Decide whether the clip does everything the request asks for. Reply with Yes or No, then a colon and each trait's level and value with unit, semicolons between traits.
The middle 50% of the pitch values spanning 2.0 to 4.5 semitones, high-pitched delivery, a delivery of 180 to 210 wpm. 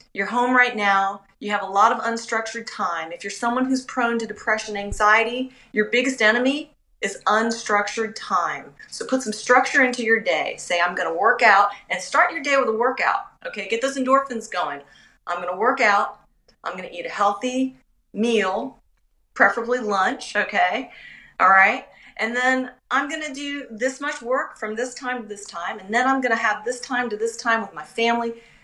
Yes: average, 3.6 semitones; high, 230 Hz; average, 200 wpm